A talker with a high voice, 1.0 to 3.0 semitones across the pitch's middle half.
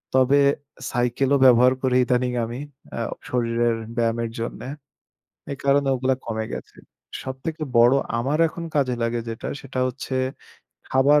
No: low, 125 Hz; narrow, 2.5 semitones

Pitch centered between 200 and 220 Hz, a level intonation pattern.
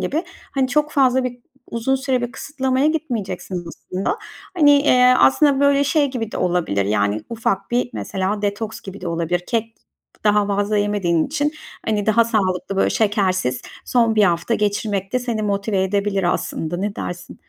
No: high, 210 Hz; average, 4.9 semitones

